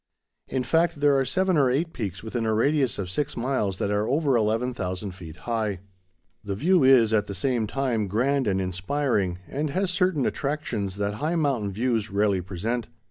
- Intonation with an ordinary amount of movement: No, wide, 5.7 semitones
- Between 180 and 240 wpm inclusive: Yes, average, 185 wpm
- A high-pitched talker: No, low, 120 Hz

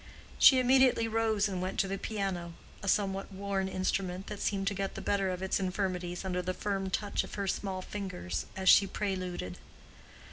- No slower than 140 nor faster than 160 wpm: No, average, 180 wpm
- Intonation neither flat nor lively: No, narrow, 1.6 semitones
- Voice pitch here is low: No, high, 195 Hz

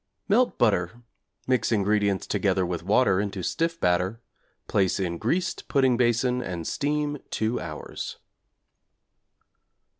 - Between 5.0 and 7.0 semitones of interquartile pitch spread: Yes, wide, 5.6 semitones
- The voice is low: Yes, low, 110 Hz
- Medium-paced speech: No, slow, 115 wpm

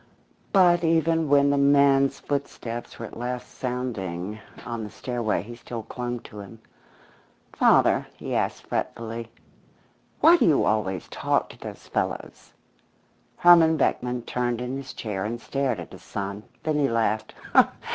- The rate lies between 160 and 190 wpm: No, average, 145 wpm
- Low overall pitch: Yes, low, 125 Hz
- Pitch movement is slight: No, average, 4.3 semitones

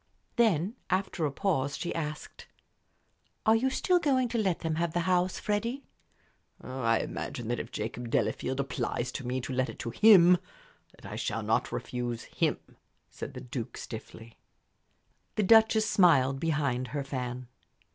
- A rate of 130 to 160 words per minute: Yes, average, 155 wpm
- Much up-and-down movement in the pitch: Yes, wide, 7.9 semitones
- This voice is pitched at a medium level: Yes, medium, 150 Hz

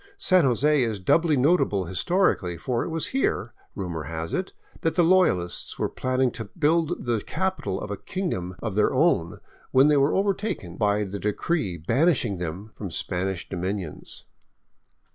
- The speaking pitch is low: Yes, low, 115 Hz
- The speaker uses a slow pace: No, average, 160 wpm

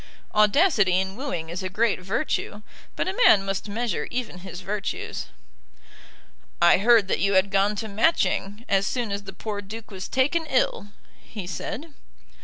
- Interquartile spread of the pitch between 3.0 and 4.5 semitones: Yes, average, 3.4 semitones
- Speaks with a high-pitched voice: Yes, high, 205 Hz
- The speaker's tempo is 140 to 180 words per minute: Yes, average, 165 wpm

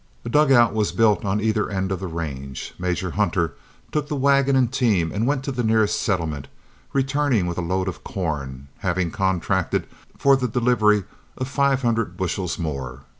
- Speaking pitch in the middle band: No, low, 105 Hz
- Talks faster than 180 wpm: No, average, 175 wpm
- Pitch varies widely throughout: Yes, wide, 6.3 semitones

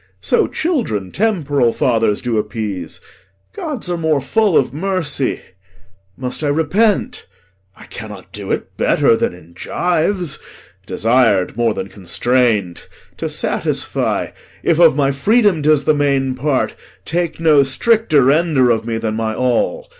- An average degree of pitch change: No, wide, 6.7 semitones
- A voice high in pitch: No, medium, 140 Hz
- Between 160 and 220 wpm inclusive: No, average, 140 wpm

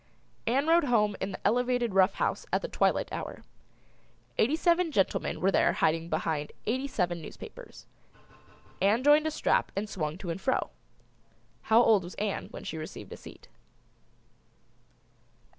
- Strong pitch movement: Yes, wide, 6.5 semitones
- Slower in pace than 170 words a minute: Yes, average, 155 wpm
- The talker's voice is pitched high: Yes, high, 210 Hz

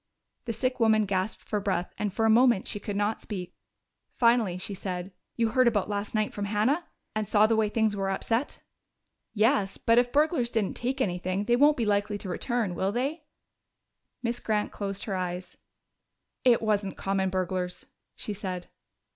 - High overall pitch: Yes, high, 210 Hz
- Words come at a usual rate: Yes, average, 180 wpm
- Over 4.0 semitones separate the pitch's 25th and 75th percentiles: No, average, 3.3 semitones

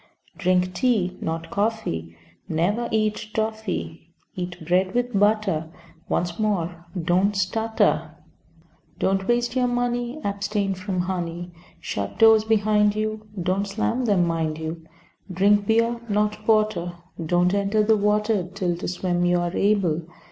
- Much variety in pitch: No, average, 3.5 semitones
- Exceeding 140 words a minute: No, slow, 135 wpm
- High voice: Yes, high, 200 Hz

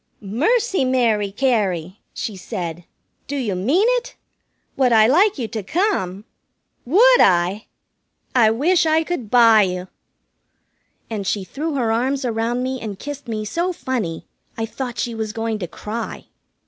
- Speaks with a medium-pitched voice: No, high, 230 Hz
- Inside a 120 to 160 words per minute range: Yes, average, 150 wpm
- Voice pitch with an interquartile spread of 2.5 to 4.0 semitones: No, average, 5.2 semitones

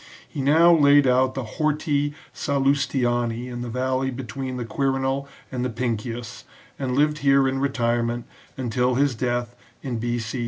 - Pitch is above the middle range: No, low, 130 Hz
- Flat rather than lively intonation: Yes, narrow, 2.3 semitones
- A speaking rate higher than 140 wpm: Yes, average, 155 wpm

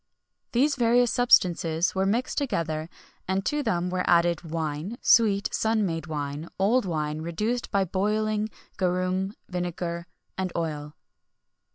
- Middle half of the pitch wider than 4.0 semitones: Yes, average, 4.5 semitones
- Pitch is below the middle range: No, medium, 185 Hz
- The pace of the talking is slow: Yes, slow, 130 wpm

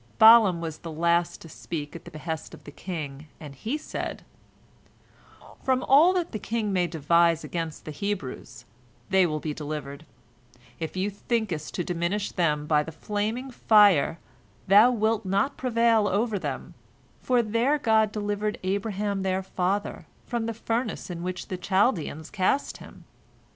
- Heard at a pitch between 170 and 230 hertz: Yes, high, 190 Hz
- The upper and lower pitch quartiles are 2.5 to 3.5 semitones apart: No, average, 5.1 semitones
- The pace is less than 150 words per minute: No, average, 155 wpm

